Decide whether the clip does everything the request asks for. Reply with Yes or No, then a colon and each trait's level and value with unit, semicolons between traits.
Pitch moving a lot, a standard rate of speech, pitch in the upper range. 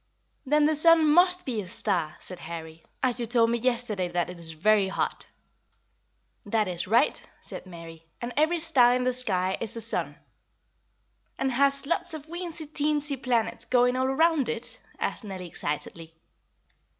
Yes: wide, 7.5 semitones; average, 165 wpm; high, 240 Hz